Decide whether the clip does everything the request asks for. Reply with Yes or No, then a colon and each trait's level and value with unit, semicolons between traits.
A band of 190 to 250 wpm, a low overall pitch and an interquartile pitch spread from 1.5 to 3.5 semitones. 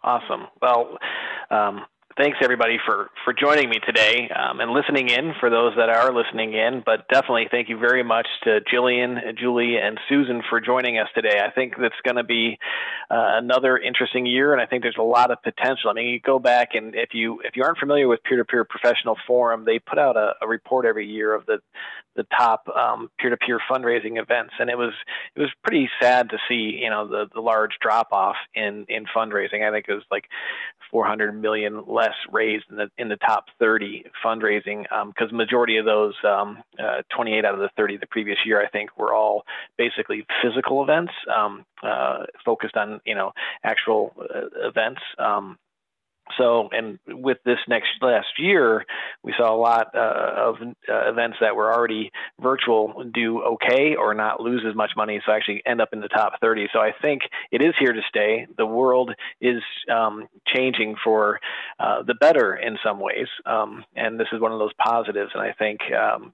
Yes: fast, 205 wpm; low, 115 Hz; narrow, 2.5 semitones